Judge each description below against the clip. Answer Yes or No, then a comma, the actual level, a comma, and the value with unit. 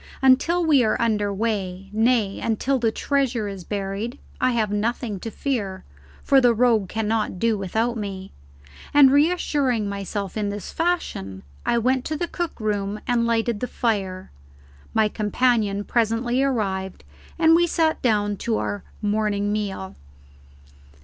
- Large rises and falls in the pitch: No, average, 3.6 semitones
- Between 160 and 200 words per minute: No, average, 145 wpm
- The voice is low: No, high, 220 Hz